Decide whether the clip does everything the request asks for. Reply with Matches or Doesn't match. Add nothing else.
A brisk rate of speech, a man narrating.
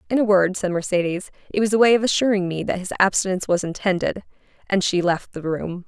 Doesn't match